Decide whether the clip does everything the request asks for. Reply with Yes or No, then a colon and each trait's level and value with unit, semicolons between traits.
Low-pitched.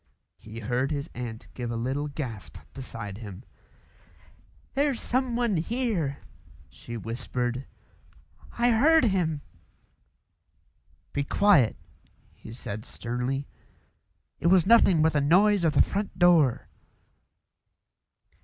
No: medium, 145 Hz